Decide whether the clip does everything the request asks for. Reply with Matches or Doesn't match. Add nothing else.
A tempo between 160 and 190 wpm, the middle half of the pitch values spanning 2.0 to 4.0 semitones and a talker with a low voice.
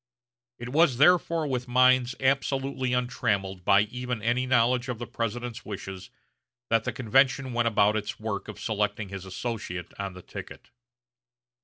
Doesn't match